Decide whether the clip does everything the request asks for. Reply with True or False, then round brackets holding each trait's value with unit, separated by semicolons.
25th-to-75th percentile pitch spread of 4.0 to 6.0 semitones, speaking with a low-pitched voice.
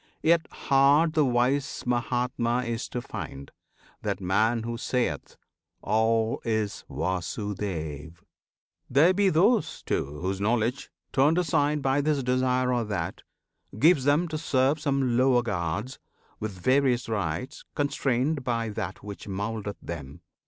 True (5.1 semitones; 120 Hz)